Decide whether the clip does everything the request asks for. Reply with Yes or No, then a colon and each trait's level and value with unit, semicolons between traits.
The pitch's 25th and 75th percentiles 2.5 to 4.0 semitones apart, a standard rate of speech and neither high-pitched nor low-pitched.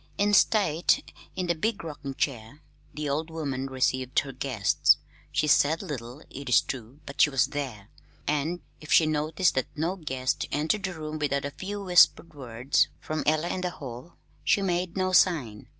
No: average, 4.4 semitones; average, 180 wpm; medium, 150 Hz